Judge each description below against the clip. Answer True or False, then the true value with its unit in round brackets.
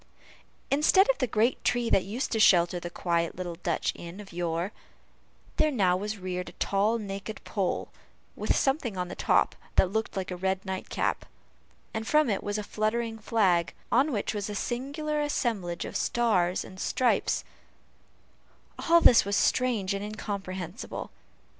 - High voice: True (205 Hz)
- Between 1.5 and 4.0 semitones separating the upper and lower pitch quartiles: False (4.4 semitones)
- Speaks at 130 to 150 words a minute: False (160 wpm)